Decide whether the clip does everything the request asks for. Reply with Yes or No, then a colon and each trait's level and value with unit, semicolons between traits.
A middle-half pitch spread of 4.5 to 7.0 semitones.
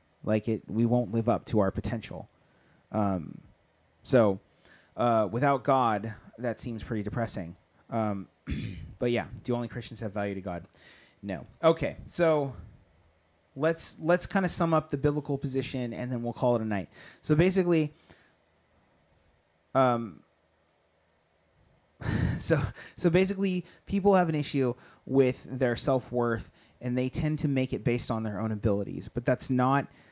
Yes: average, 5.2 semitones